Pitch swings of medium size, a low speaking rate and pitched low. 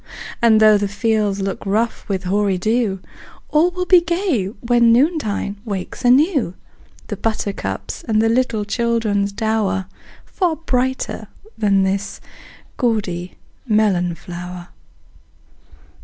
No: average, 3.6 semitones; slow, 110 wpm; high, 215 Hz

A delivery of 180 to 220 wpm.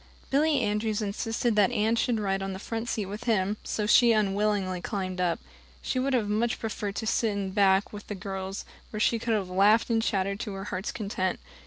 Yes: fast, 205 wpm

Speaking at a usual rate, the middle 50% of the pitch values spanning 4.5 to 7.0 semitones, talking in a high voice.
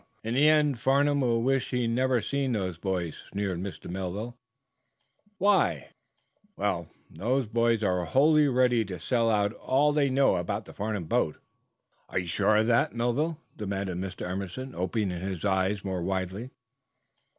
No: average, 160 wpm; wide, 5.5 semitones; low, 110 Hz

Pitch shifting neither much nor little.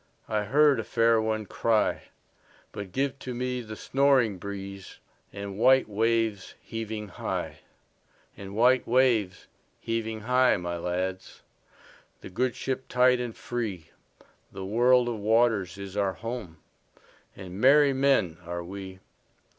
Yes: average, 4.3 semitones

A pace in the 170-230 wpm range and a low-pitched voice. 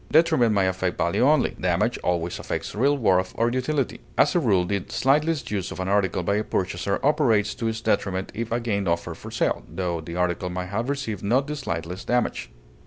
Yes: average, 200 wpm; low, 105 Hz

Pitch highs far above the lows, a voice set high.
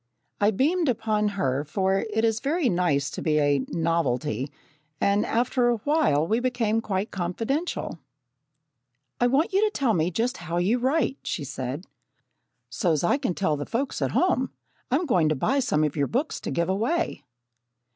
Yes: wide, 7.9 semitones; high, 210 Hz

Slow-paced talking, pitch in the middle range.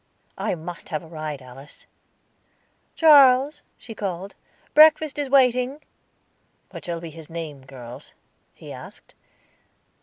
Yes: slow, 120 wpm; medium, 175 Hz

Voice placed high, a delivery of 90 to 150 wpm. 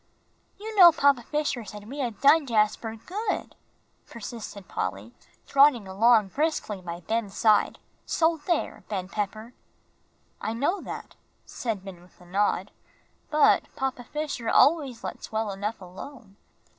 Yes: high, 225 Hz; slow, 135 wpm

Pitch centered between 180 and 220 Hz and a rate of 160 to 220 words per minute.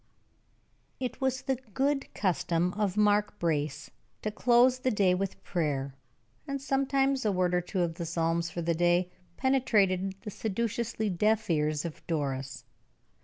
No: high, 190 Hz; average, 150 wpm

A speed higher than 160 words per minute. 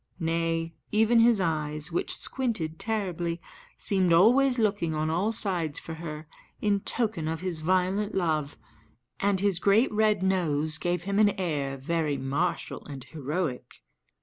No: average, 145 wpm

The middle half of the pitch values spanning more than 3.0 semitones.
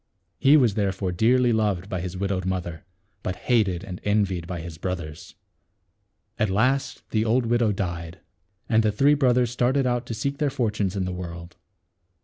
Yes: average, 5.0 semitones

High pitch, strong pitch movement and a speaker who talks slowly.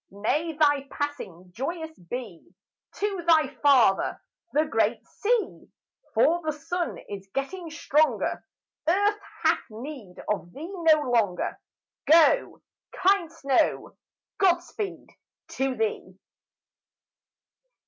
Yes: very high, 300 Hz; wide, 6.6 semitones; slow, 105 wpm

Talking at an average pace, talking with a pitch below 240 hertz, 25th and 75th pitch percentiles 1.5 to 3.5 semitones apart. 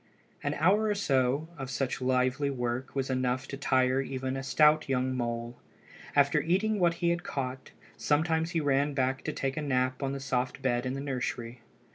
Yes: average, 190 wpm; low, 135 Hz; narrow, 2.6 semitones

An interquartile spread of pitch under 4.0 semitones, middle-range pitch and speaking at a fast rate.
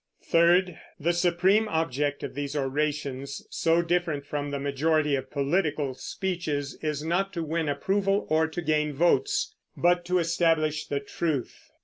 No: average, 3.3 semitones; medium, 155 Hz; average, 145 wpm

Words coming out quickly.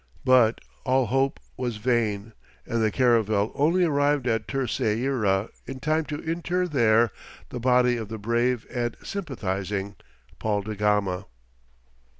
No: slow, 135 wpm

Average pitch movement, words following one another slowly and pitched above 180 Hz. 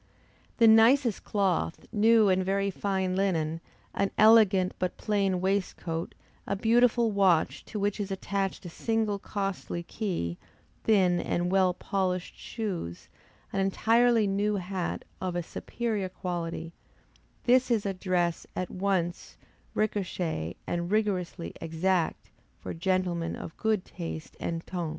Yes: average, 3.0 semitones; slow, 130 wpm; high, 190 Hz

